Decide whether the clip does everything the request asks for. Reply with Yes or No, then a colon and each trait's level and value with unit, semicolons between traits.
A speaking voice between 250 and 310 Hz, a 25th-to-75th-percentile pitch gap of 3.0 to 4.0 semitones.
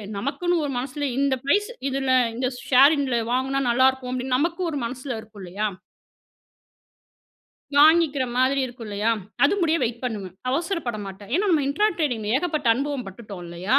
Yes: very high, 260 Hz; average, 3.7 semitones